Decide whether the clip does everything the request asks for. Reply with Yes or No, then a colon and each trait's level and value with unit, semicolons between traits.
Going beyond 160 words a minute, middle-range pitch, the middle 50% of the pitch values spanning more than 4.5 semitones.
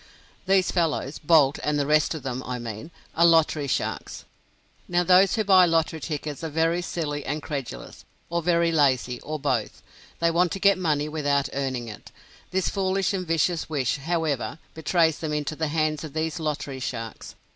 No: average, 180 wpm; medium, 155 Hz; average, 3.1 semitones